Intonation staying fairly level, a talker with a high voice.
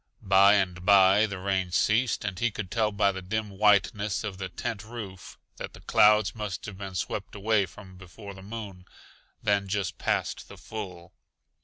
No: narrow, 2.0 semitones; low, 100 Hz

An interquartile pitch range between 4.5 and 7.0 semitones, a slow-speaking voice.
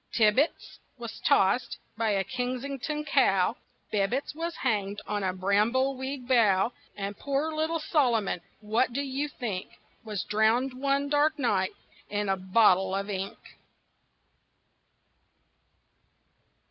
Yes: wide, 5.5 semitones; slow, 115 wpm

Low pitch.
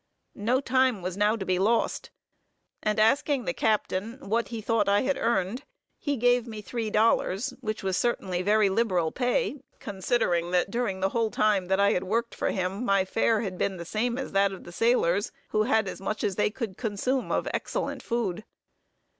No: high, 215 Hz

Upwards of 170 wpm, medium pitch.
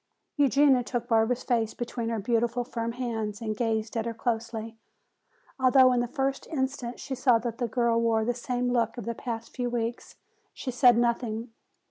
No: average, 180 wpm; high, 235 Hz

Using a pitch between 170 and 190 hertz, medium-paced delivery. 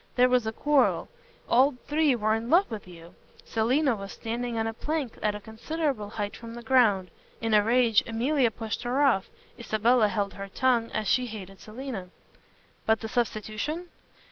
No: high, 230 Hz; average, 175 wpm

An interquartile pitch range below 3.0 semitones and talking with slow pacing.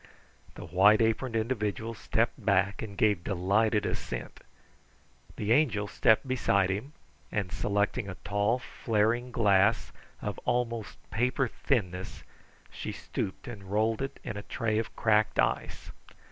Yes: narrow, 2.6 semitones; slow, 130 wpm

